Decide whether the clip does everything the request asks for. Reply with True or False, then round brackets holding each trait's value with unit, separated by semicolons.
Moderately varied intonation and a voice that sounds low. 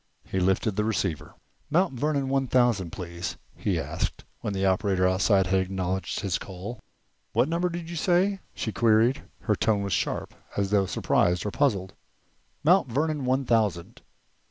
False (6.2 semitones; 105 Hz)